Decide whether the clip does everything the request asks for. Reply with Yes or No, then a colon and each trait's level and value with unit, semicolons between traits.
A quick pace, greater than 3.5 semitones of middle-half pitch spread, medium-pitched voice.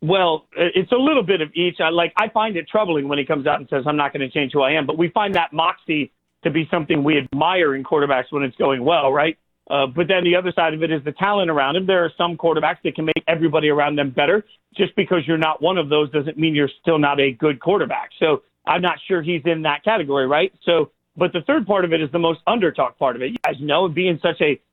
No: fast, 270 wpm; average, 3.2 semitones; medium, 165 Hz